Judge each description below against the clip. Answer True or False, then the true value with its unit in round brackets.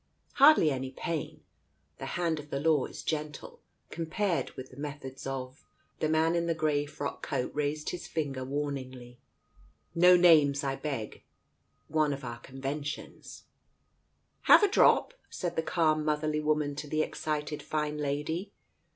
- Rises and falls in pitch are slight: True (2.3 semitones)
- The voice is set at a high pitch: False (150 Hz)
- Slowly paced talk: False (165 wpm)